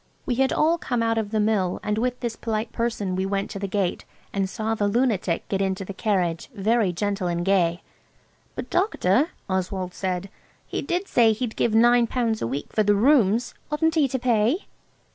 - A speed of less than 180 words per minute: No, average, 200 wpm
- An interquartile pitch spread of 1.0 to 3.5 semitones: No, average, 3.9 semitones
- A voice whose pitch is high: Yes, high, 215 Hz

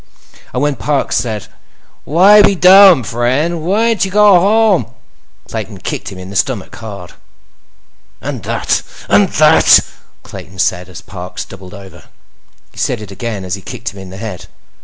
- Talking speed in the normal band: Yes, average, 160 wpm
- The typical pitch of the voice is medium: No, low, 120 Hz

